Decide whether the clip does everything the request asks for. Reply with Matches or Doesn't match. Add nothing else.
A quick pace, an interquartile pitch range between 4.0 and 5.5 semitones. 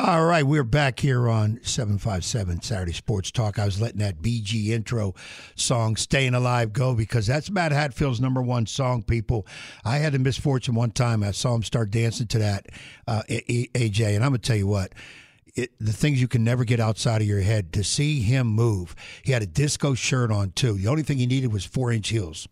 Doesn't match